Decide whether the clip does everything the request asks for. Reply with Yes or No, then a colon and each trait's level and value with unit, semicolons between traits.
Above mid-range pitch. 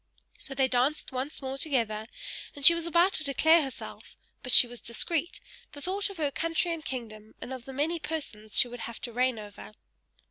Yes: very high, 270 Hz